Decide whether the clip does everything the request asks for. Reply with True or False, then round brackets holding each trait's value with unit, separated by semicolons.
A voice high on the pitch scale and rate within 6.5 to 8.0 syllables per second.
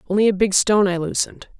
True (195 Hz; 7.5 syllables/s)